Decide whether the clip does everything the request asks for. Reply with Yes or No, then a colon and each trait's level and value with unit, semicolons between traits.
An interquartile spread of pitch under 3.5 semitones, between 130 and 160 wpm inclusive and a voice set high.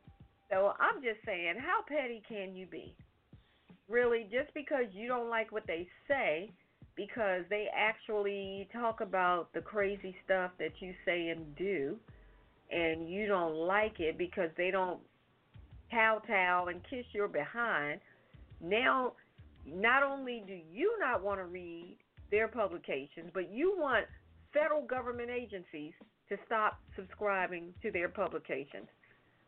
No: average, 4.6 semitones; average, 140 wpm; high, 195 Hz